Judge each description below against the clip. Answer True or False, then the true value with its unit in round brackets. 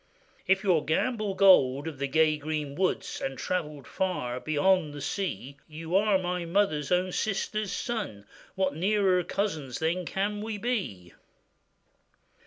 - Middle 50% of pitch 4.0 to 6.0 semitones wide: True (4.8 semitones)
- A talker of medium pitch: True (180 Hz)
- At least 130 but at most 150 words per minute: True (145 wpm)